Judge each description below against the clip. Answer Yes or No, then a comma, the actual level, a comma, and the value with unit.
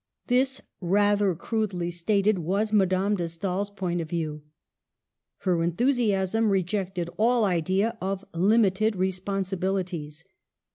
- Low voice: No, high, 190 Hz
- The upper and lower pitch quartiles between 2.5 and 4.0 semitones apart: Yes, average, 3.0 semitones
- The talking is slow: Yes, slow, 115 wpm